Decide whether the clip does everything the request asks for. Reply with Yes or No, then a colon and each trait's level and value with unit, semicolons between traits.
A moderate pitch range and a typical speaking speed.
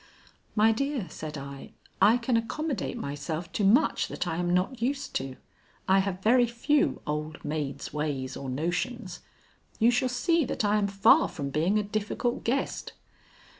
No: wide, 7.5 semitones; average, 165 wpm